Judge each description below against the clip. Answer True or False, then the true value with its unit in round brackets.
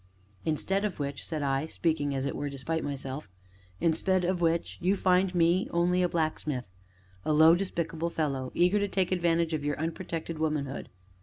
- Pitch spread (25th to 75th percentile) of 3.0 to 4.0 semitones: True (3.5 semitones)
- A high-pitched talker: False (165 Hz)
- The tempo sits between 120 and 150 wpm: False (170 wpm)